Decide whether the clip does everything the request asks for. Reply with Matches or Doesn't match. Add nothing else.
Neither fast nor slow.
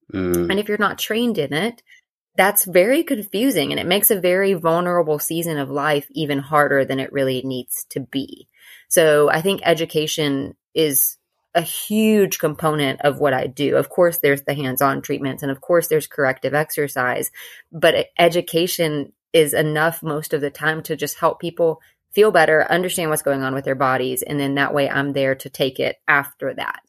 Matches